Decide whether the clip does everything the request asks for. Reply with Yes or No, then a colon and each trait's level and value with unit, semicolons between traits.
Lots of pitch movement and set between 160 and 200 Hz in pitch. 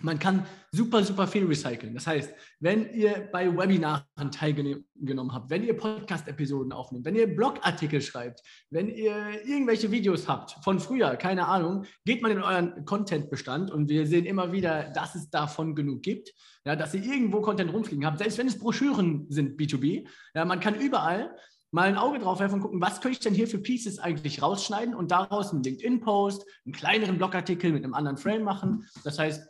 Yes: wide, 5.7 semitones; medium, 185 Hz